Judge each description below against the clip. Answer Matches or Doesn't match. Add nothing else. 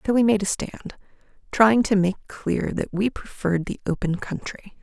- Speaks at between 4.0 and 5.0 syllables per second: Matches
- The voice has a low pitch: Doesn't match